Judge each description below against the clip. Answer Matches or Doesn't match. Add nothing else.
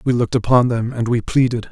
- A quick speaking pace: Matches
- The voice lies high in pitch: Doesn't match